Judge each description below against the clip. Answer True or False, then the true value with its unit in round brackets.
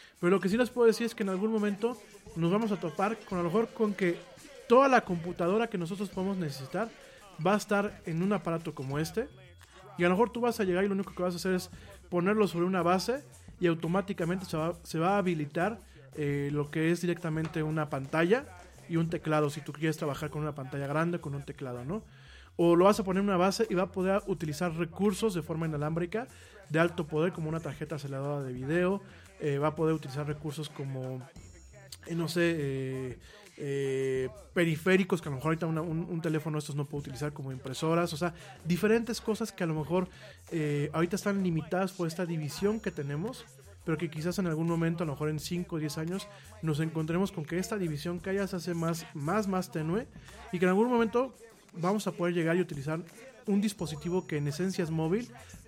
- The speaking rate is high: True (220 wpm)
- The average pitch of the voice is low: False (170 Hz)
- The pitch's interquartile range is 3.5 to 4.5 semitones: True (4.1 semitones)